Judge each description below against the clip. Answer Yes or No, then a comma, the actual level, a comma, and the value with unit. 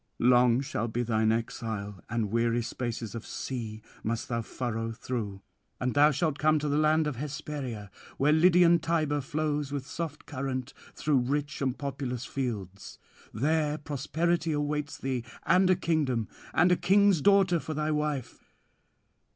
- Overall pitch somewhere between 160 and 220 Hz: No, medium, 140 Hz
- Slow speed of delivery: No, average, 150 wpm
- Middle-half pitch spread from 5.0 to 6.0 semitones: No, average, 4.6 semitones